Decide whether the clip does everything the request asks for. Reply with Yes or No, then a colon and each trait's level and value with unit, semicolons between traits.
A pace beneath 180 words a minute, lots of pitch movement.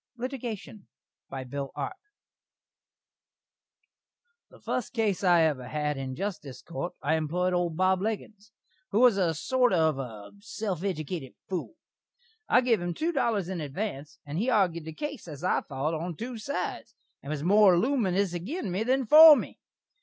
Yes: average, 165 wpm; wide, 6.0 semitones